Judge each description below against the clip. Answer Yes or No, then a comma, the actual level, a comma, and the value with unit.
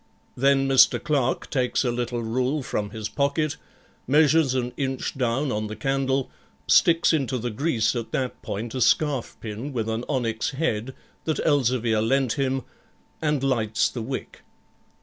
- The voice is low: Yes, low, 130 Hz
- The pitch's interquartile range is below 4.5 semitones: Yes, average, 3.2 semitones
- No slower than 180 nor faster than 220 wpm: No, average, 155 wpm